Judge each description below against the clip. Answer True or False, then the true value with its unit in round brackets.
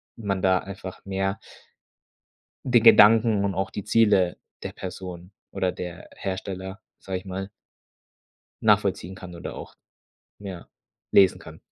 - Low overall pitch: True (95 Hz)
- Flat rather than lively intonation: True (1.5 semitones)